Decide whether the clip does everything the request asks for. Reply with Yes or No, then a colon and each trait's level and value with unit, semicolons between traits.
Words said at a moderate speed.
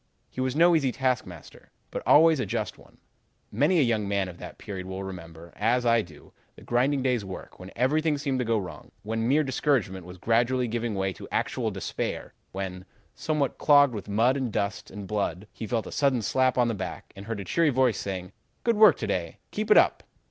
No: fast, 215 wpm